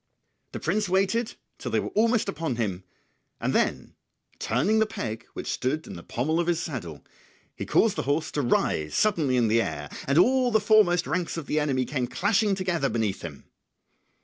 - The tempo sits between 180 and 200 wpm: Yes, average, 185 wpm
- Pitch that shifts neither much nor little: No, wide, 8.5 semitones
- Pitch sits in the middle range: Yes, medium, 160 Hz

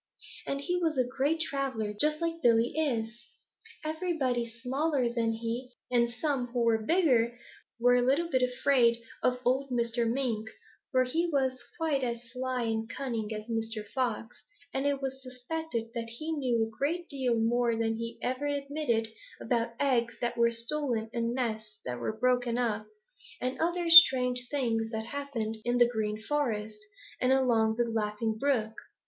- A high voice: Yes, high, 245 Hz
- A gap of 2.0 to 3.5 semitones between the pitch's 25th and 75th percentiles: Yes, average, 3.2 semitones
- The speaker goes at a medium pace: Yes, average, 165 wpm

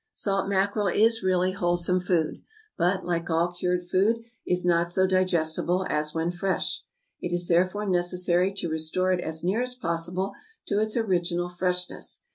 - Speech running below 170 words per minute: Yes, average, 160 wpm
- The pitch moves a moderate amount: No, narrow, 1.6 semitones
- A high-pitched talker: No, medium, 180 Hz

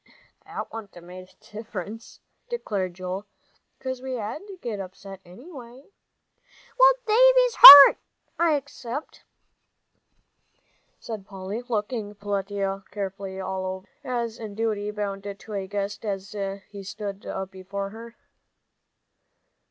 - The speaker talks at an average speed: No, slow, 120 wpm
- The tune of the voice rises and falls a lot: No, average, 3.4 semitones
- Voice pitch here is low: No, high, 205 Hz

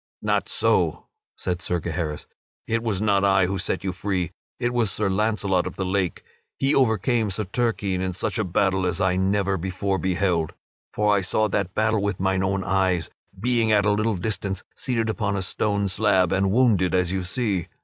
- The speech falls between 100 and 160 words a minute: No, average, 190 wpm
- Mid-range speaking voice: No, very low, 95 Hz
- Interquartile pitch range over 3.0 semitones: No, narrow, 2.6 semitones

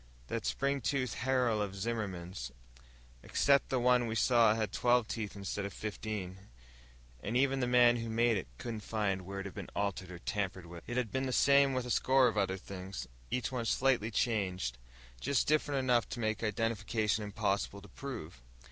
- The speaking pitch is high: No, low, 110 Hz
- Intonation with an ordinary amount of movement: Yes, average, 4.1 semitones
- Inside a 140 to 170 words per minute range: No, average, 185 wpm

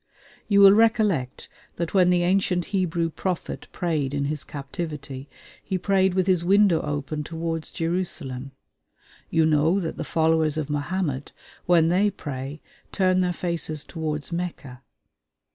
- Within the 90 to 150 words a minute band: Yes, average, 140 wpm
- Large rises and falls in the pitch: No, average, 3.7 semitones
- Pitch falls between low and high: Yes, medium, 165 Hz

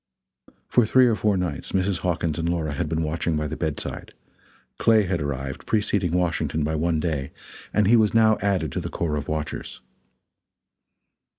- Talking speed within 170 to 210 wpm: Yes, average, 175 wpm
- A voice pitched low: Yes, very low, 85 Hz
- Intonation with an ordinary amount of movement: Yes, average, 4.5 semitones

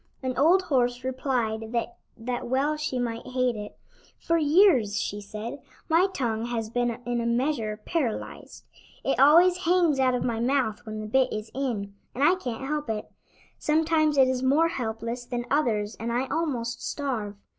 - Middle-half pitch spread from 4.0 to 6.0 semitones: Yes, average, 4.3 semitones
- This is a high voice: Yes, very high, 250 Hz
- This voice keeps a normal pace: Yes, average, 170 wpm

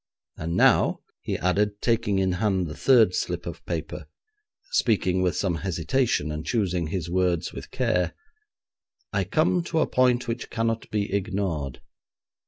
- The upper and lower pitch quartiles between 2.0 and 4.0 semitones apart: No, average, 4.4 semitones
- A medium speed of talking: Yes, average, 150 wpm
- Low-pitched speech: Yes, very low, 95 Hz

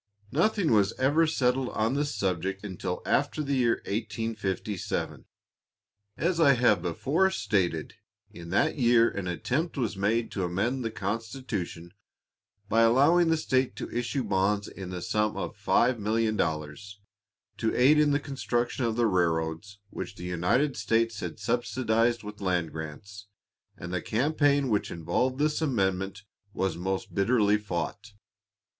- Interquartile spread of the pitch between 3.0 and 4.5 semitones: No, average, 5.2 semitones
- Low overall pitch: Yes, low, 110 Hz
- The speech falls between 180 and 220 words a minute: No, average, 140 wpm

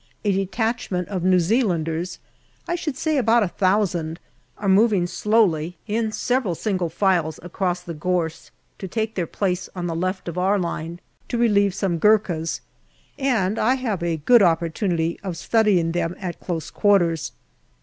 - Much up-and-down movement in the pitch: No, average, 3.9 semitones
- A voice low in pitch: No, medium, 185 Hz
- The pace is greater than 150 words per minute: Yes, average, 170 wpm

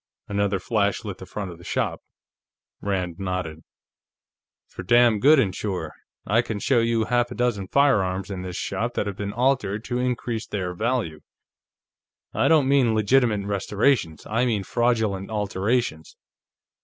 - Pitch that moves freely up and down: No, average, 4.1 semitones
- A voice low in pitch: Yes, low, 105 Hz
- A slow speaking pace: No, average, 155 wpm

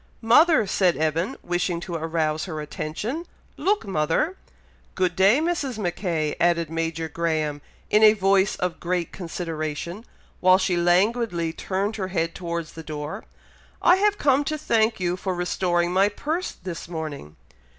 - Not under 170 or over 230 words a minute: No, average, 150 wpm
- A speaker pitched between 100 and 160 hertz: No, medium, 180 Hz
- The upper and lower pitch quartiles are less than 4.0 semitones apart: No, average, 4.4 semitones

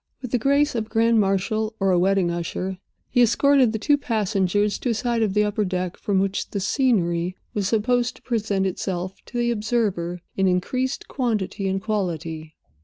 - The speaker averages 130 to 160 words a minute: No, average, 185 wpm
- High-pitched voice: Yes, high, 210 Hz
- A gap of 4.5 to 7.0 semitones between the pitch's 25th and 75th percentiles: No, average, 3.8 semitones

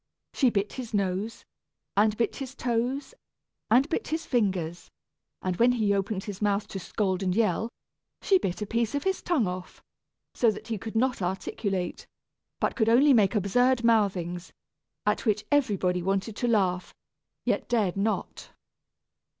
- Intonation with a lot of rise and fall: No, average, 3.8 semitones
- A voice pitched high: Yes, high, 215 Hz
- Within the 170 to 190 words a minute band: No, average, 160 wpm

